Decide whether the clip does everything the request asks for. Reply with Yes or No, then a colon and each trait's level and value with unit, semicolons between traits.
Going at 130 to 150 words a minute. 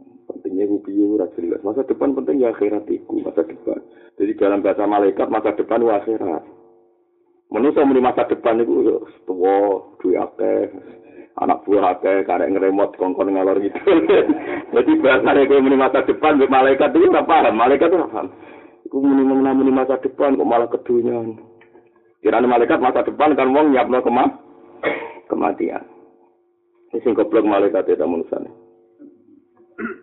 Yes: fast, 140 wpm